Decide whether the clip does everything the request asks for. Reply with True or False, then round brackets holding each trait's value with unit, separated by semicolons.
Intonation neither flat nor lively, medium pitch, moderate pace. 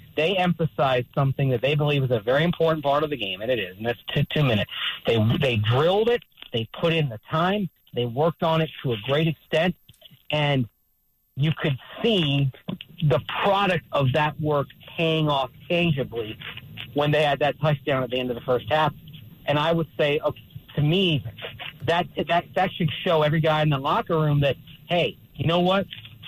True (4.1 semitones; 150 Hz; 195 wpm)